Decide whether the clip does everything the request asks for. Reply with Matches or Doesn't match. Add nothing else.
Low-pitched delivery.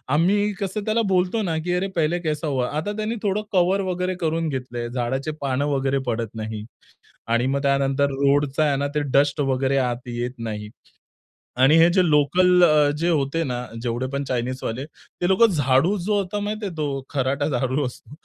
Doesn't match